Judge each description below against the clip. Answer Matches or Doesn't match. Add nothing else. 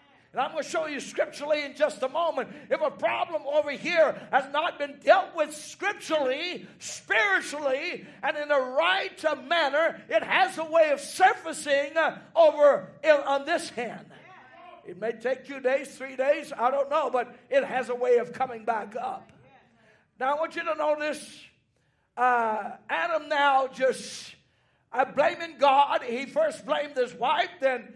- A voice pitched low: Doesn't match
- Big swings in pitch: Doesn't match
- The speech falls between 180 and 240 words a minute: Doesn't match